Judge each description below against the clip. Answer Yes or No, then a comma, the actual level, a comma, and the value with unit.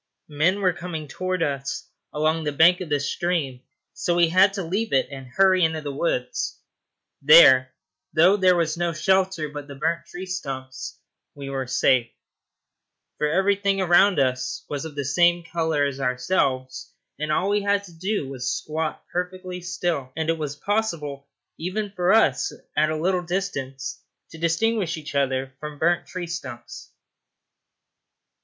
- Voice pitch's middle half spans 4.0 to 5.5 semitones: Yes, average, 4.6 semitones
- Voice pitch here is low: No, medium, 160 Hz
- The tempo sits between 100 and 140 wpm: No, average, 160 wpm